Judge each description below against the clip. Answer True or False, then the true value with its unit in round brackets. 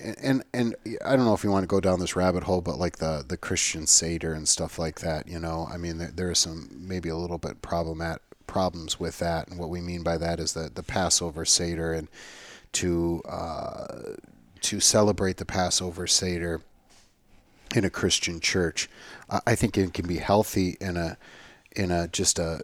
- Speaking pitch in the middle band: False (85 Hz)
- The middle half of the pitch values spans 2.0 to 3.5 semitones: True (2.4 semitones)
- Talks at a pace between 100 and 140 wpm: False (200 wpm)